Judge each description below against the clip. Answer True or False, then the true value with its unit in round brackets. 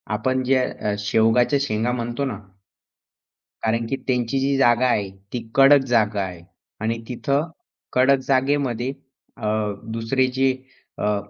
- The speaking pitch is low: True (120 Hz)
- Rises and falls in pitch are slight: False (3.3 semitones)